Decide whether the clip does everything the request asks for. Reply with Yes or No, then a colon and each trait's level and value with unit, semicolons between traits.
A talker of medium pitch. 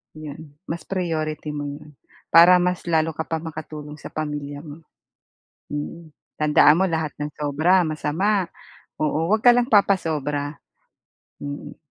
Yes: medium, 155 Hz